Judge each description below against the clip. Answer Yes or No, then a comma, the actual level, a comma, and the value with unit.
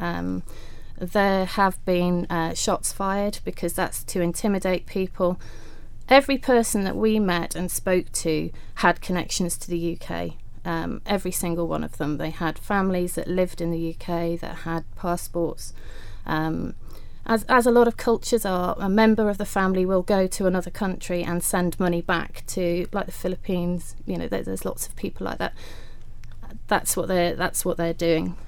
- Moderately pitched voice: Yes, medium, 175 Hz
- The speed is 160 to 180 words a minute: Yes, average, 175 wpm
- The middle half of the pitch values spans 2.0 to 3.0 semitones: Yes, average, 2.7 semitones